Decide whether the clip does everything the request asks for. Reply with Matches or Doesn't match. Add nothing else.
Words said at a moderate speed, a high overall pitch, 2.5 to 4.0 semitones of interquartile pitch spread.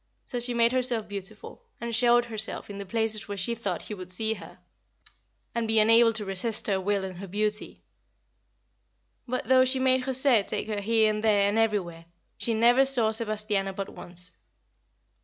Matches